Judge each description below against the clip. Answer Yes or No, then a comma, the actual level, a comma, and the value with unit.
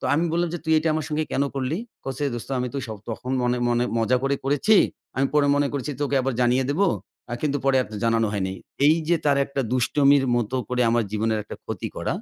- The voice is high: No, low, 135 Hz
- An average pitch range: Yes, average, 3.2 semitones